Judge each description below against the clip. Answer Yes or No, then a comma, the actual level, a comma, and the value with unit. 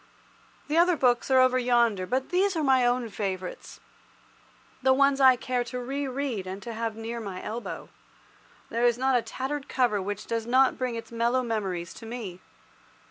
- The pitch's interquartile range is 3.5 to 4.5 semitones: No, average, 2.8 semitones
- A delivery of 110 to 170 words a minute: No, average, 180 wpm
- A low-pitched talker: No, high, 245 Hz